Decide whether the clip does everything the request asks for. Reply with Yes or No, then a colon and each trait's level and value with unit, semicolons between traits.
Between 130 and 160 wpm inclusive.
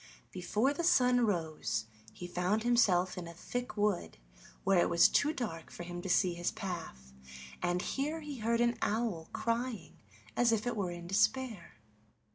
No: average, 170 wpm